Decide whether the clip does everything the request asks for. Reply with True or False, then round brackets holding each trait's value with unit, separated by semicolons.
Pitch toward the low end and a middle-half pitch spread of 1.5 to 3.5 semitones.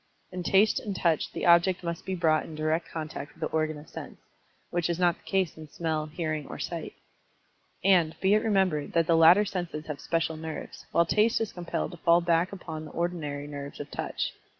False (170 Hz; 2.5 semitones)